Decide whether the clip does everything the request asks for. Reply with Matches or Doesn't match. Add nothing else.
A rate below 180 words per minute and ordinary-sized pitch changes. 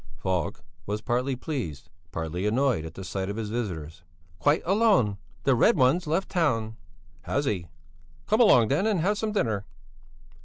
Doesn't match